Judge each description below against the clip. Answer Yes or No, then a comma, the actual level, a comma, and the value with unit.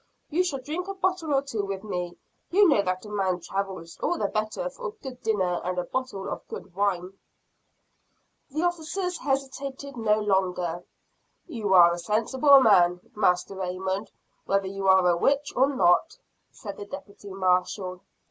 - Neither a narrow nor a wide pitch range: No, wide, 7.0 semitones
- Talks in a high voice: Yes, high, 205 Hz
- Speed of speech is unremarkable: Yes, average, 165 wpm